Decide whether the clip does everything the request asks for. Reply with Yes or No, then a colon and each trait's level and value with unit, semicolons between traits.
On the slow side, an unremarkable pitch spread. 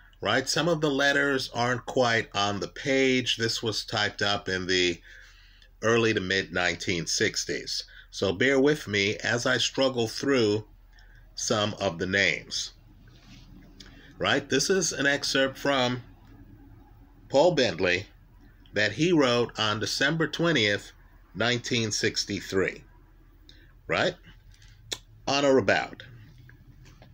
Yes: slow, 115 wpm; average, 4.7 semitones